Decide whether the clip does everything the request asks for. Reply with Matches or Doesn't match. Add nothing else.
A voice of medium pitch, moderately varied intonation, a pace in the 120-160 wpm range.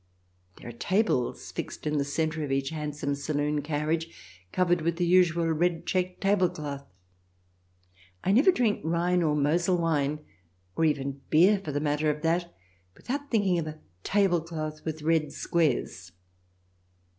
Matches